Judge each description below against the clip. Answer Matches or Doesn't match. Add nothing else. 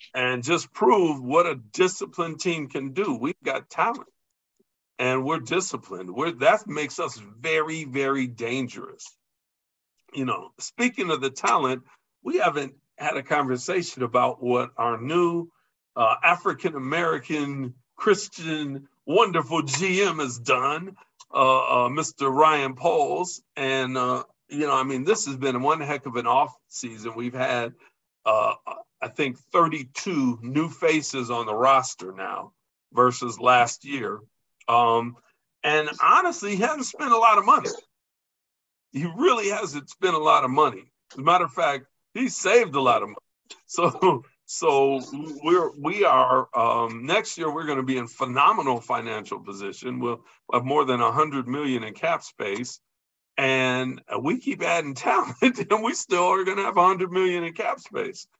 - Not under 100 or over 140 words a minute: Doesn't match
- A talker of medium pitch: Matches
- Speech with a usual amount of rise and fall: Doesn't match